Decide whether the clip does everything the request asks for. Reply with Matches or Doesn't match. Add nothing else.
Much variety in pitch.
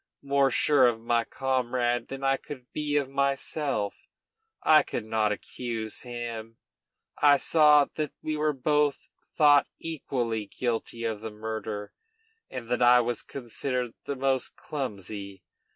Doesn't match